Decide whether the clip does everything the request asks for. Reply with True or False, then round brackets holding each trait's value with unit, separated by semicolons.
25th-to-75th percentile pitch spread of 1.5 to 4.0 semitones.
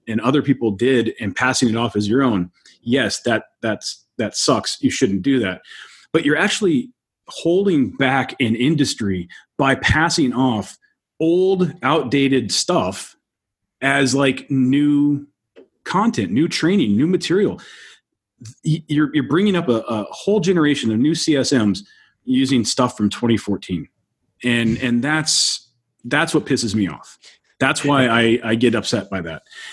False (4.7 semitones)